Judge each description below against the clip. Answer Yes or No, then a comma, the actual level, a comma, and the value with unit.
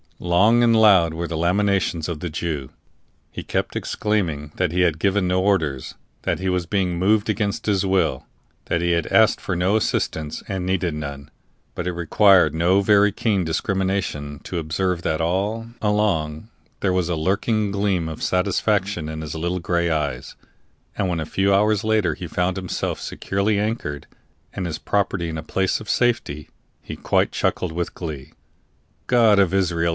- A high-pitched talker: No, very low, 90 Hz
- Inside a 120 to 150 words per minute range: No, average, 175 wpm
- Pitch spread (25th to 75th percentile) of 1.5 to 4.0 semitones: Yes, average, 3.5 semitones